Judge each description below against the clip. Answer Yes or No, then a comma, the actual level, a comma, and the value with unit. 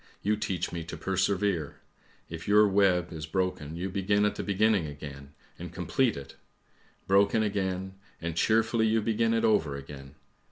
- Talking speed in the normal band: Yes, average, 165 wpm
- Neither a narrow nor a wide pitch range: Yes, average, 4.3 semitones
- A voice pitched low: Yes, very low, 95 Hz